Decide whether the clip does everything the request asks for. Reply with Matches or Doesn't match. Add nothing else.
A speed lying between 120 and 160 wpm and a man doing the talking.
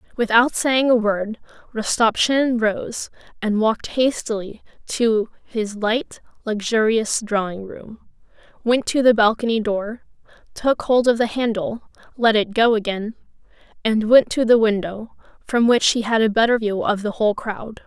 Doesn't match